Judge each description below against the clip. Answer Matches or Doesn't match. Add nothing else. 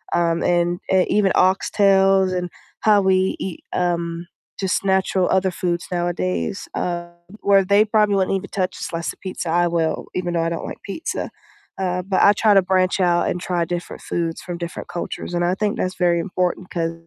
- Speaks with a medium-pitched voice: Matches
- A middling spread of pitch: Doesn't match